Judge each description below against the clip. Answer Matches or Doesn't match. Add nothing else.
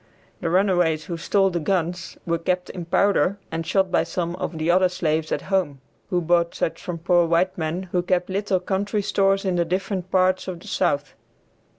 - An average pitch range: Doesn't match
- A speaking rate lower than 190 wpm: Doesn't match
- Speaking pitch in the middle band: Matches